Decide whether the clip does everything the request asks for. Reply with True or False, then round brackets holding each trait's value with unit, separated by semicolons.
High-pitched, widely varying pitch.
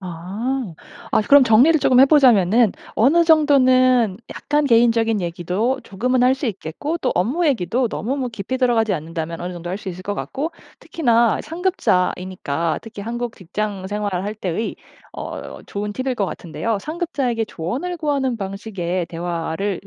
True (225 Hz; 5.9 semitones)